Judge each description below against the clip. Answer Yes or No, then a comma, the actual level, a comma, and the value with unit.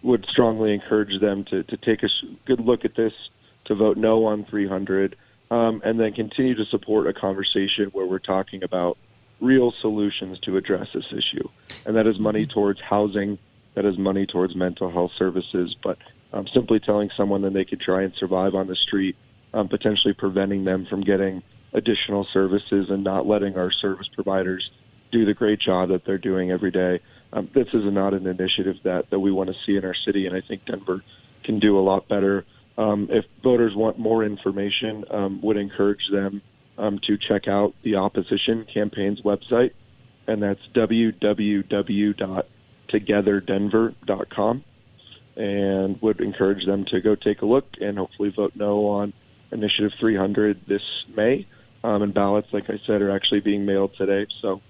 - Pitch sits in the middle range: No, low, 100 Hz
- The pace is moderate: Yes, average, 175 wpm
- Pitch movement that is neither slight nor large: No, narrow, 1.9 semitones